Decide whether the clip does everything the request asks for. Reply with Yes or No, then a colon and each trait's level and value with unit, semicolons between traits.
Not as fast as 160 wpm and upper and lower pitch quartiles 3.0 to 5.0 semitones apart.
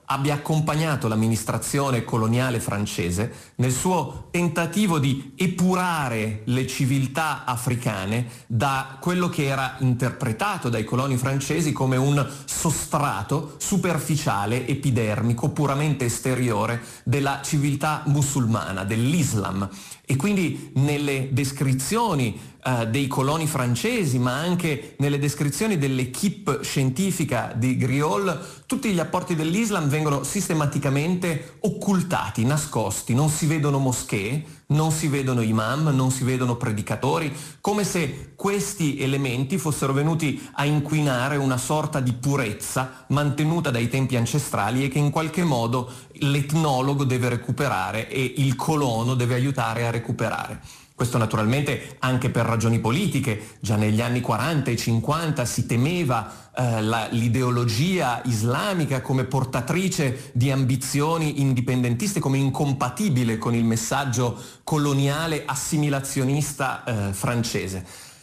Yes: slow, 115 wpm; average, 3.6 semitones